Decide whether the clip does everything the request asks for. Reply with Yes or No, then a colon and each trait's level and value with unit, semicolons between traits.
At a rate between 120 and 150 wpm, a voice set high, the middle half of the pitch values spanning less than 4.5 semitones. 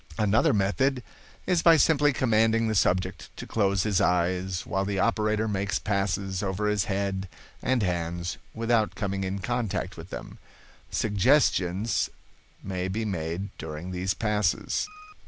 No: average, 140 wpm; low, 100 Hz; average, 3.0 semitones